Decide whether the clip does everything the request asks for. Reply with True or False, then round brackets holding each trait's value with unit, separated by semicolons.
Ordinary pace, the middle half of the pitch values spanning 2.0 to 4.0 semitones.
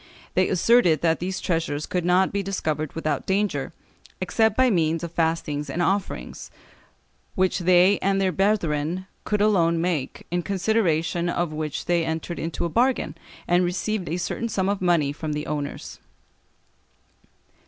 True (155 wpm; 3.3 semitones)